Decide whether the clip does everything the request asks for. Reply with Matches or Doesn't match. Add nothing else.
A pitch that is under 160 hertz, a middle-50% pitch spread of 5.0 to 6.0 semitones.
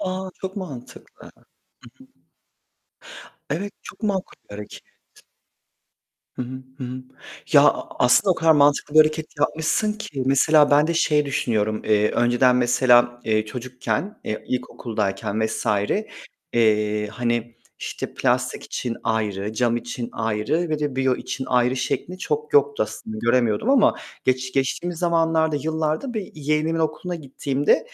Matches